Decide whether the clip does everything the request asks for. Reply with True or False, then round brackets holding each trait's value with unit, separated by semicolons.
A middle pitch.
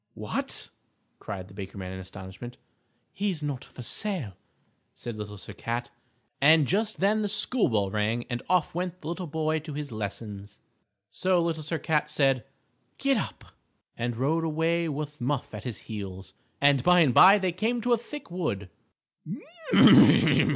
True (145 Hz)